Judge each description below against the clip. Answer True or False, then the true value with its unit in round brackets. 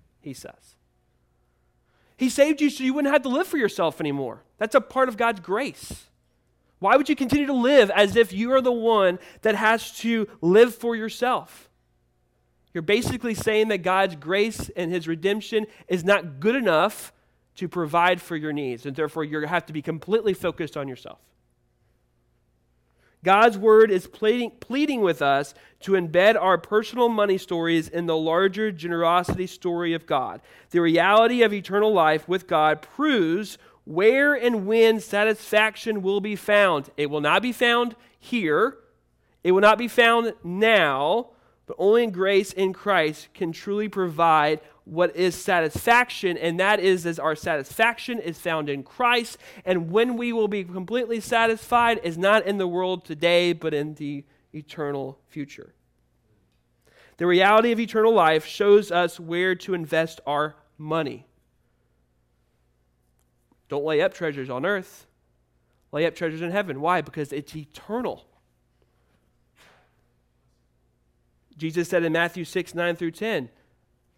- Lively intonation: True (6.3 semitones)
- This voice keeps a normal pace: True (150 wpm)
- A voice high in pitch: False (180 Hz)